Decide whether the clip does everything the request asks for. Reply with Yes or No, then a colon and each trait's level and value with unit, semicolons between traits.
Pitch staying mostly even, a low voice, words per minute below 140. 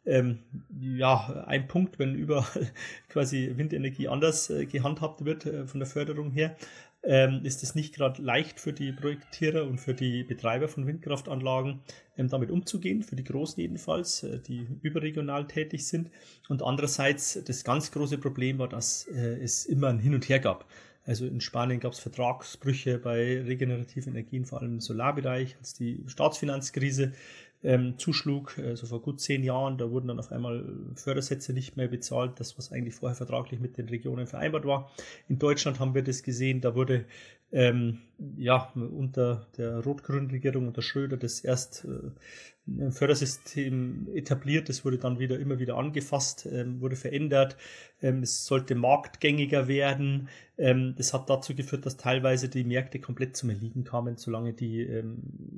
No: narrow, 2.1 semitones; low, 130 Hz; average, 160 wpm